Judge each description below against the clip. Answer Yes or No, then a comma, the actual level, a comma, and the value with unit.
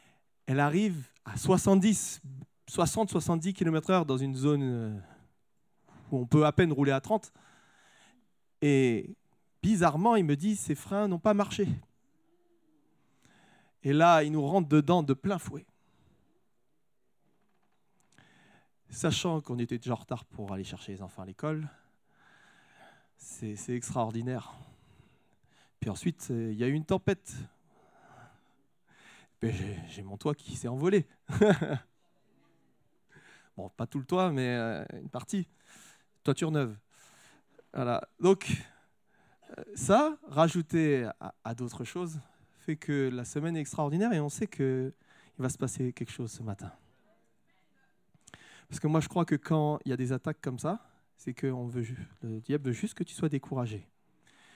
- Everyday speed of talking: No, slow, 135 wpm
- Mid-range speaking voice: Yes, medium, 145 Hz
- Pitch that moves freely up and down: Yes, wide, 6.1 semitones